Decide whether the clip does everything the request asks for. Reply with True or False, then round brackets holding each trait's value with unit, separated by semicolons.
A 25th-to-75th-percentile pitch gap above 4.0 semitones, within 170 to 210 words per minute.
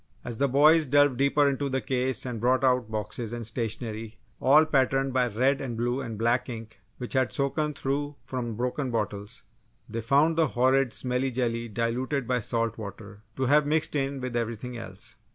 False (2.9 semitones; 185 wpm)